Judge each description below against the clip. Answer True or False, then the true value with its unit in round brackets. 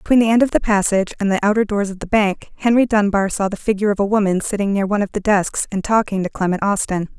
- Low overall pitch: False (200 Hz)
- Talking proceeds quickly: True (265 wpm)